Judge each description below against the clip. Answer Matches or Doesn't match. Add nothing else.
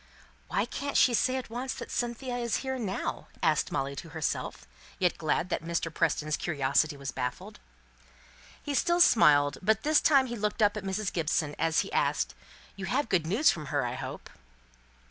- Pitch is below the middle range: Doesn't match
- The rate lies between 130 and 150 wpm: Doesn't match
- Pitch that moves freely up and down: Matches